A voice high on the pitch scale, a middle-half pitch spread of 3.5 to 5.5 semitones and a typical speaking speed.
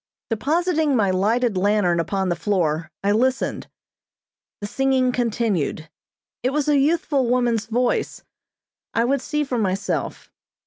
No: high, 235 Hz; average, 5.2 semitones; slow, 130 wpm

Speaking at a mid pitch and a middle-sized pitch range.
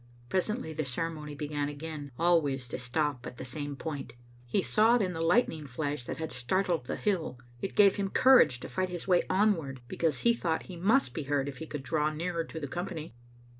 Yes: medium, 160 Hz; average, 4.2 semitones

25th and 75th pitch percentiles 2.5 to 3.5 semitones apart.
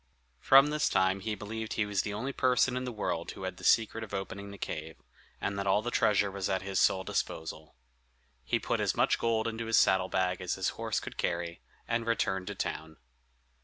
Yes: average, 3.2 semitones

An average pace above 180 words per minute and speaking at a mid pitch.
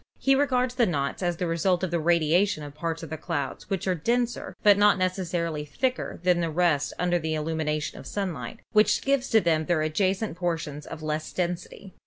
Yes: fast, 205 wpm; medium, 175 Hz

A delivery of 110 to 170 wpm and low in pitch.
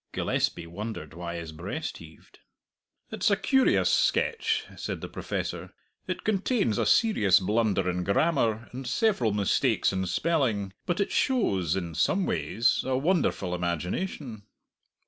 Yes: slow, 135 wpm; low, 110 Hz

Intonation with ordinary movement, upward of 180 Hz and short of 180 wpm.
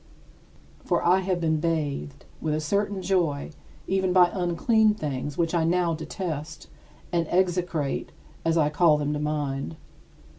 No: average, 3.3 semitones; medium, 165 Hz; average, 145 wpm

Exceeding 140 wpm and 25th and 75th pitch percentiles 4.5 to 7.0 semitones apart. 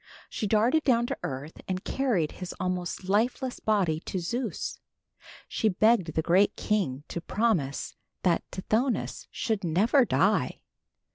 No: slow, 135 wpm; average, 5.1 semitones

